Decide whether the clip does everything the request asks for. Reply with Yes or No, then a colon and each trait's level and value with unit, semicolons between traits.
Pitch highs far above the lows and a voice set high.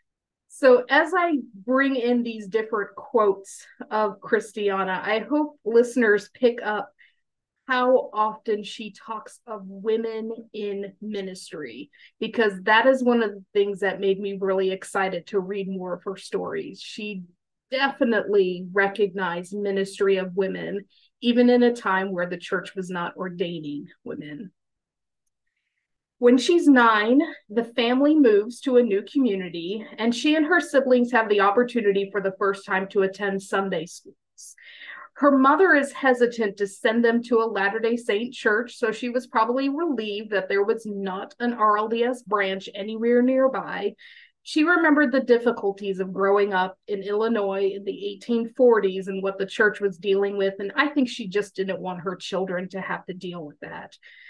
No: average, 3.9 semitones; high, 210 Hz